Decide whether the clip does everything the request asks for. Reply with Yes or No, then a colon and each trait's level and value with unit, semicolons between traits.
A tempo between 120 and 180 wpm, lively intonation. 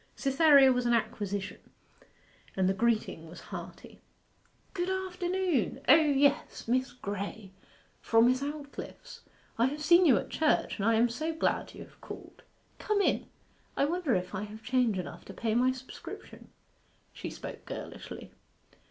Yes: average, 150 wpm; wide, 5.8 semitones